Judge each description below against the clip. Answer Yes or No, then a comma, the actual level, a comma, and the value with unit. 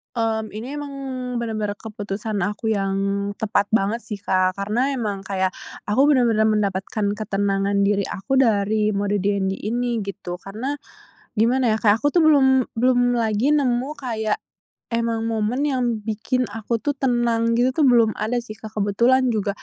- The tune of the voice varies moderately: Yes, average, 3.2 semitones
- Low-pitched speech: No, high, 220 Hz